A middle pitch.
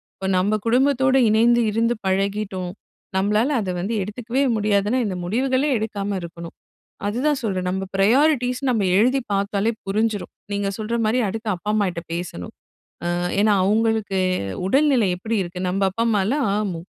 No: high, 210 Hz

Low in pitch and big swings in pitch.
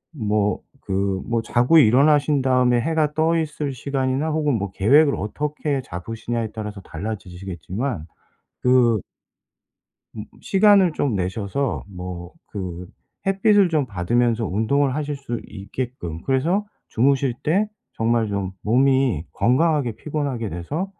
Yes: low, 125 Hz; wide, 6.0 semitones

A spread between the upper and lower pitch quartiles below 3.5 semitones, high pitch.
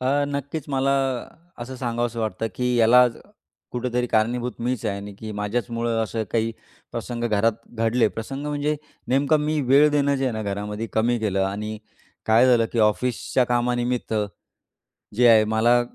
No: narrow, 2.5 semitones; low, 120 Hz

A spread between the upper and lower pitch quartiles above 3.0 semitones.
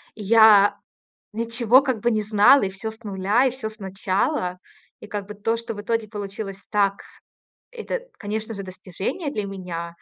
No: average, 2.7 semitones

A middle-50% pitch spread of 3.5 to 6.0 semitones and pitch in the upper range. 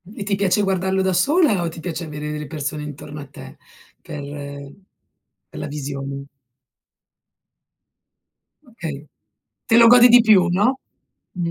No: wide, 5.5 semitones; medium, 175 Hz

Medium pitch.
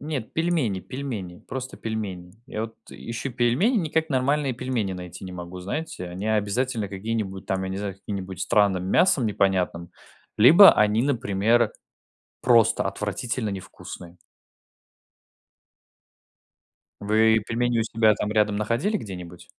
No: low, 110 Hz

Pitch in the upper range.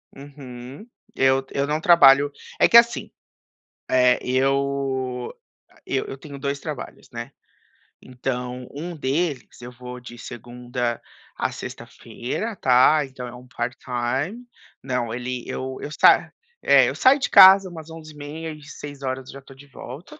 No: low, 135 Hz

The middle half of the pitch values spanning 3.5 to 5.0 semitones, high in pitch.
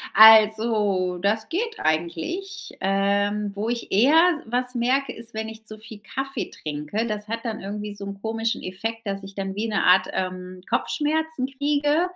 Yes: average, 4.0 semitones; high, 220 Hz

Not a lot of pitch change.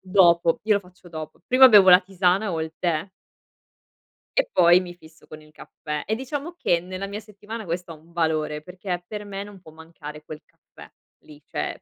No: average, 4.0 semitones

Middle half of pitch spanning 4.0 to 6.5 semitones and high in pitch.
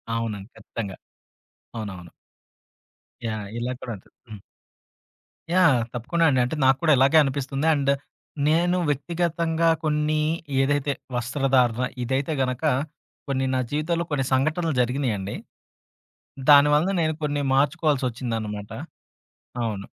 No: average, 4.5 semitones; low, 135 Hz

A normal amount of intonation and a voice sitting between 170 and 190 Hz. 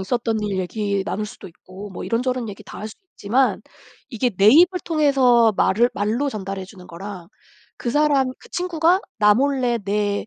No: average, 4.9 semitones; high, 225 Hz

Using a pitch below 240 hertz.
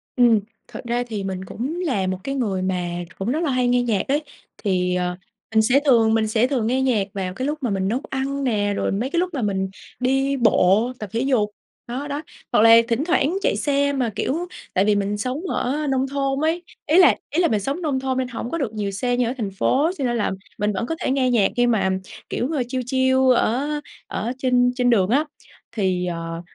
No: high, 245 Hz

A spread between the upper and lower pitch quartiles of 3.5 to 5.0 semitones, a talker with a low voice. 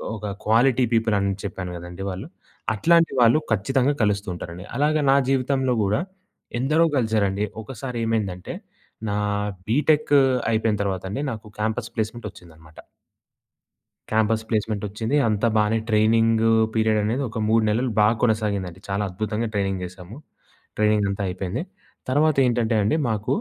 No: average, 3.1 semitones; low, 110 Hz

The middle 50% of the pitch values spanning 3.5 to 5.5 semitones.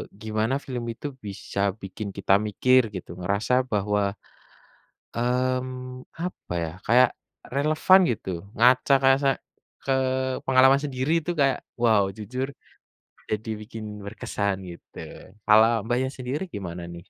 Yes: average, 4.1 semitones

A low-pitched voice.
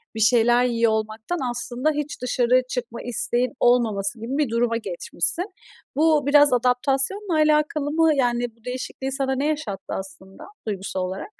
No: very high, 250 Hz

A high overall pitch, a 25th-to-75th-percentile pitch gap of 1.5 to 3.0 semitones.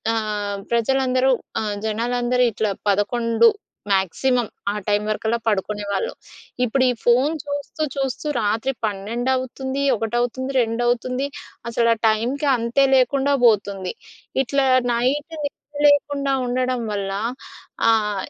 No: high, 240 Hz; average, 3.7 semitones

